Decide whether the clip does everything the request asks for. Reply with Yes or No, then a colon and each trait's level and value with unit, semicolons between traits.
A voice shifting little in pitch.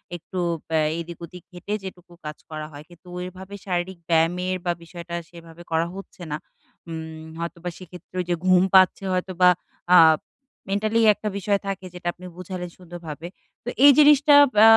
Yes: narrow, 2.0 semitones